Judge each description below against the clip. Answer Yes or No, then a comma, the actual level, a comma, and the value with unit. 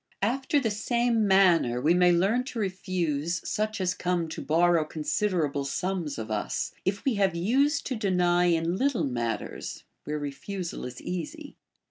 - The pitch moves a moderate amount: Yes, average, 4.8 semitones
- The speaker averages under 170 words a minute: Yes, average, 155 wpm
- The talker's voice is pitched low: No, medium, 180 Hz